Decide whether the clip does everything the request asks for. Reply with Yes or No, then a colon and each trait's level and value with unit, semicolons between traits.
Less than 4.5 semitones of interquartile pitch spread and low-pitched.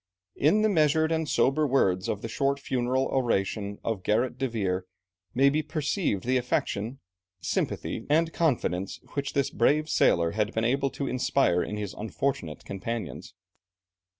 No: average, 5.3 semitones; low, 125 Hz